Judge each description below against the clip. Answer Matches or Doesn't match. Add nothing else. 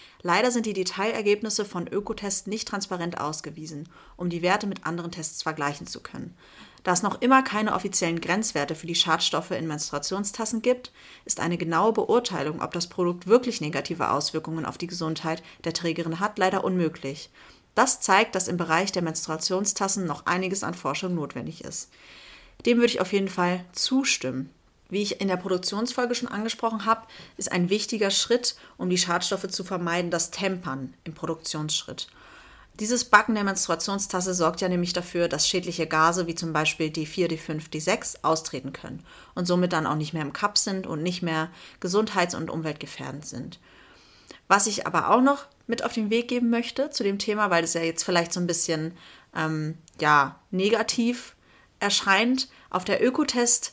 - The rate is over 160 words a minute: Matches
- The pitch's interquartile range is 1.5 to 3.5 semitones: Doesn't match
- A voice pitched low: Doesn't match